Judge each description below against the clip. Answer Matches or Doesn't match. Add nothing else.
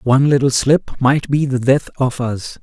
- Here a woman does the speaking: Doesn't match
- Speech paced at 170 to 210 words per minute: Matches